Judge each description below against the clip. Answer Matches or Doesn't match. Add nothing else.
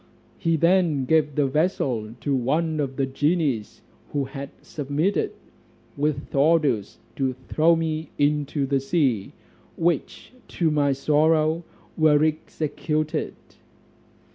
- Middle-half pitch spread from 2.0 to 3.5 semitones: Matches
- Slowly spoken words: Matches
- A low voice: Doesn't match